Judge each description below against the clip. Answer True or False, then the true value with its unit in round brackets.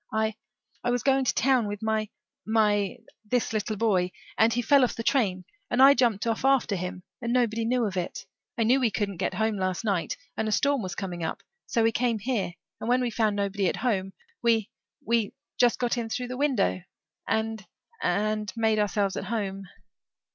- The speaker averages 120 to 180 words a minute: False (200 wpm)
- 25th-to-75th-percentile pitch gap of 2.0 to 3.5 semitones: True (3.1 semitones)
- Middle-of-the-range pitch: False (220 Hz)